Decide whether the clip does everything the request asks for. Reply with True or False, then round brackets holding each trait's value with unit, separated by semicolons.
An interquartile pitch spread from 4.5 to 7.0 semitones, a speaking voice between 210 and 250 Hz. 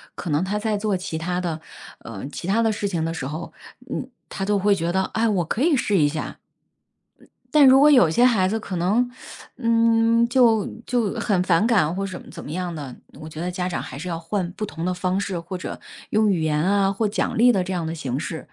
False (4.8 semitones; 190 Hz)